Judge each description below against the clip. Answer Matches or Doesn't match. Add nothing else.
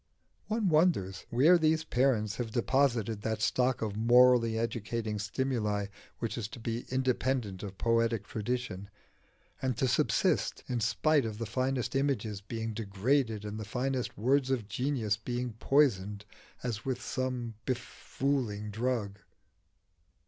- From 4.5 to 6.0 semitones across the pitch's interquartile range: Doesn't match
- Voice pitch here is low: Matches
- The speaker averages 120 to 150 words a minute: Matches